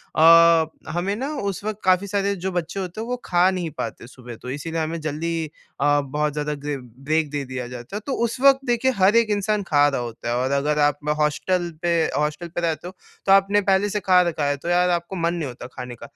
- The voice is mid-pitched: Yes, medium, 170 Hz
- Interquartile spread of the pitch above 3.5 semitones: Yes, average, 4.7 semitones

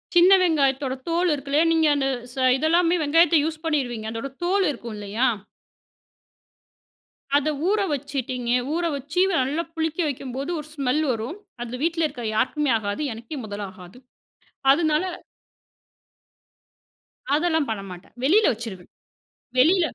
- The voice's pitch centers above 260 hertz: Yes, very high, 285 Hz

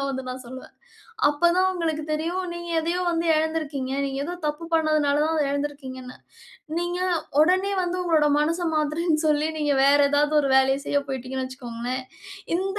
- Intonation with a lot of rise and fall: No, average, 3.6 semitones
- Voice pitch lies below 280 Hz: No, very high, 300 Hz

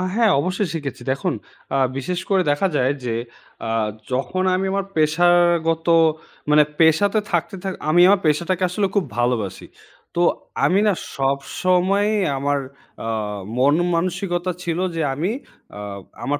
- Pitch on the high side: No, medium, 170 Hz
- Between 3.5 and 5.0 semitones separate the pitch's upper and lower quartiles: Yes, average, 4.3 semitones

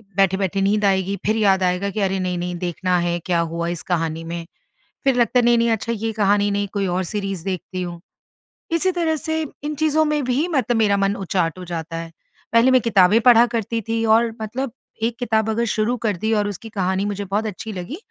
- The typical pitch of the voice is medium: No, high, 205 Hz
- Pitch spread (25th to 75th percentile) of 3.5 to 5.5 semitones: Yes, average, 3.9 semitones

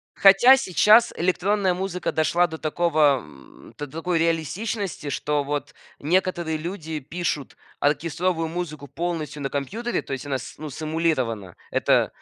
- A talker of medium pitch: Yes, medium, 160 Hz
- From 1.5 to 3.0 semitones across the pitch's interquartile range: No, average, 3.7 semitones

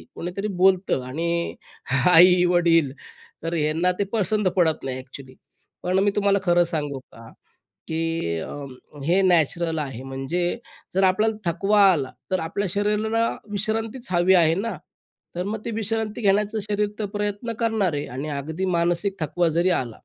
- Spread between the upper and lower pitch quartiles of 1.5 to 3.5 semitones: No, average, 4.2 semitones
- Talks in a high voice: No, medium, 180 Hz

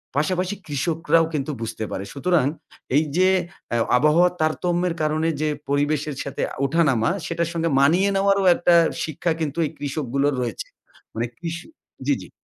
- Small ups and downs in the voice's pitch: No, average, 3.5 semitones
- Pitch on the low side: No, medium, 155 Hz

